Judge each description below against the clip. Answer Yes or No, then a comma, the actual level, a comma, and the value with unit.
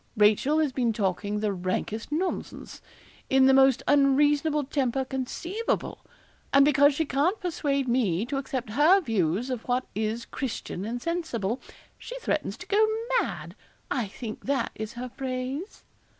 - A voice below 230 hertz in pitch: No, very high, 265 Hz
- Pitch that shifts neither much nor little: Yes, average, 4.5 semitones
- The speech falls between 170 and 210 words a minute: No, average, 150 wpm